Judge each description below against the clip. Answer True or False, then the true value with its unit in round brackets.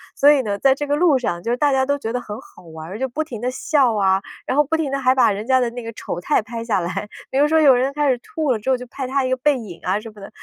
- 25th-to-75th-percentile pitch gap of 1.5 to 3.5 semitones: False (4.7 semitones)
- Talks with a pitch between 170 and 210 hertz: False (255 Hz)